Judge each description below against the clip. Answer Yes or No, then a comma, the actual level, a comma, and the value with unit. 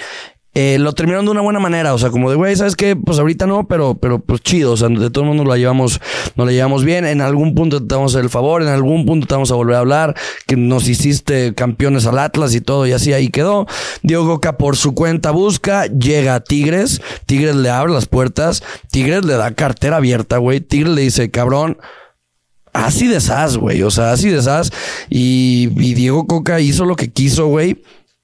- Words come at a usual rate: No, fast, 220 wpm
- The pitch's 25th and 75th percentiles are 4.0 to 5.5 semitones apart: Yes, average, 4.6 semitones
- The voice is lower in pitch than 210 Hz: Yes, medium, 140 Hz